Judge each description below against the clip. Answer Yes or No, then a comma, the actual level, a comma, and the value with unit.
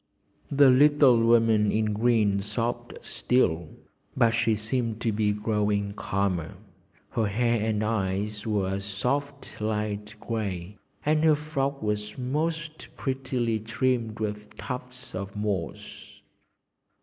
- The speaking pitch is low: Yes, low, 110 Hz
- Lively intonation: No, average, 3.3 semitones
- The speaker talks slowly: Yes, slow, 120 wpm